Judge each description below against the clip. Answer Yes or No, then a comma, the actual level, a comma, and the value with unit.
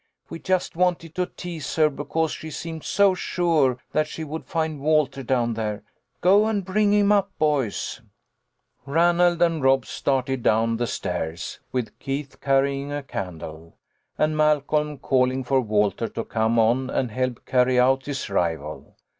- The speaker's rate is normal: Yes, average, 170 wpm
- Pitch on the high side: No, medium, 140 Hz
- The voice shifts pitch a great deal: No, average, 4.8 semitones